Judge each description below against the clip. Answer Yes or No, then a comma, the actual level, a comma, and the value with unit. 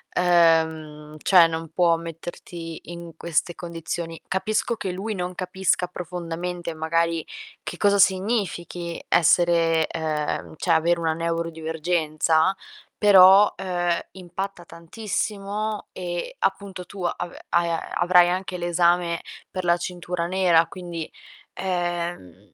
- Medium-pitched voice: Yes, medium, 175 Hz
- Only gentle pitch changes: Yes, narrow, 1.8 semitones